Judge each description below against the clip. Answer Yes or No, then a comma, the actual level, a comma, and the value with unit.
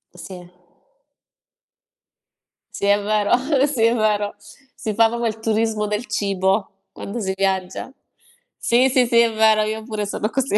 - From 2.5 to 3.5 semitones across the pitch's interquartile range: No, narrow, 2.1 semitones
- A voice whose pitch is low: No, high, 215 Hz